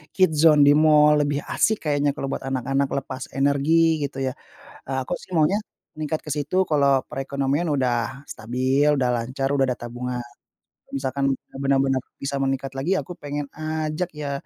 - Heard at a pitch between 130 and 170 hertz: Yes, medium, 140 Hz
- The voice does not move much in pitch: Yes, narrow, 2.2 semitones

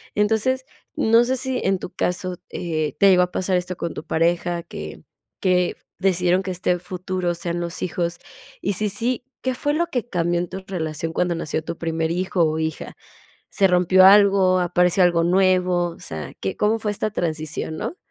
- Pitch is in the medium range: Yes, medium, 180 Hz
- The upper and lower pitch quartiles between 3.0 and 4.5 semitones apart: No, narrow, 2.4 semitones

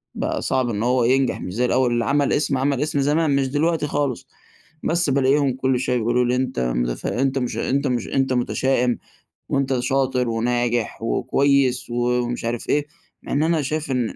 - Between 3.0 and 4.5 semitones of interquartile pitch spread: No, narrow, 2.4 semitones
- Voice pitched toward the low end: Yes, low, 130 Hz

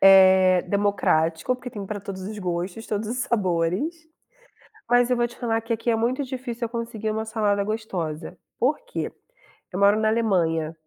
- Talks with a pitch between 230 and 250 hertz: No, high, 215 Hz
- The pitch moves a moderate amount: Yes, average, 3.9 semitones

